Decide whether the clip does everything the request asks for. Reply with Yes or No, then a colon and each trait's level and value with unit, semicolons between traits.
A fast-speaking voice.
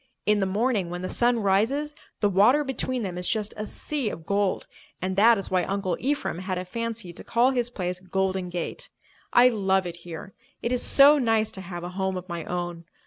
Yes: fast, 215 wpm